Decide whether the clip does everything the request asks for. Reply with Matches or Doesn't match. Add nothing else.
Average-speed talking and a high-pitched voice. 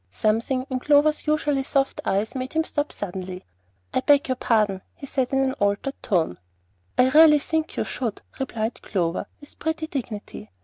Matches